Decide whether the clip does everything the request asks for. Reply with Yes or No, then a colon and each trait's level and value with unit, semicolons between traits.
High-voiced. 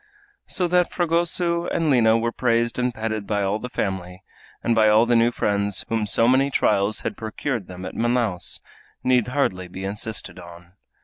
No: low, 115 Hz